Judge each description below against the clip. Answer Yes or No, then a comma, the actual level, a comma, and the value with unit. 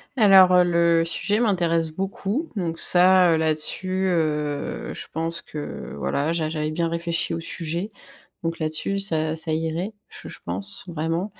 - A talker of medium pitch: Yes, medium, 170 Hz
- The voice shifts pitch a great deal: No, average, 2.8 semitones